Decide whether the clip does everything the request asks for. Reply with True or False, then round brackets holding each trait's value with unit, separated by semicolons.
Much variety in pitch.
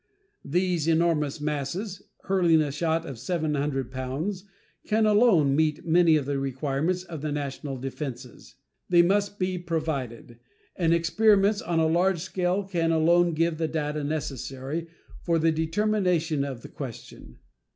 False (3.9 semitones)